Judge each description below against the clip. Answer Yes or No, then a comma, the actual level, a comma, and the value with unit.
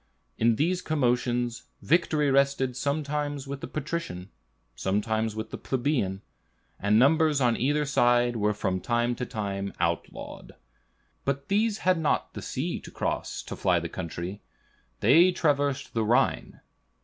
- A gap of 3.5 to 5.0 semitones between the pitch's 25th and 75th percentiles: No, wide, 5.4 semitones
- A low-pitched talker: Yes, low, 125 Hz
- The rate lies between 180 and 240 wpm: No, average, 140 wpm